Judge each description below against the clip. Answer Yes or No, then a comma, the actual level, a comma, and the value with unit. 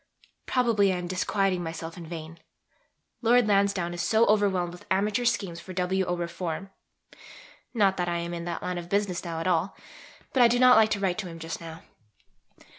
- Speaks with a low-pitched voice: No, medium, 185 Hz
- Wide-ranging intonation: No, average, 3.0 semitones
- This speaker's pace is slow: No, average, 195 wpm